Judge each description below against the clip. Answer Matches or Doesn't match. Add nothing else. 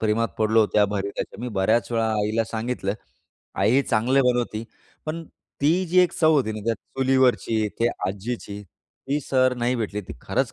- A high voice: Doesn't match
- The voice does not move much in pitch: Doesn't match